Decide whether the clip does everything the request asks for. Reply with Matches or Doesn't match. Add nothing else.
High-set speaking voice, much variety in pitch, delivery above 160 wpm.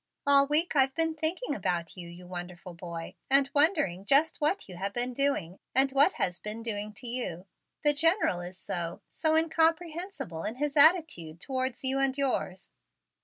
Matches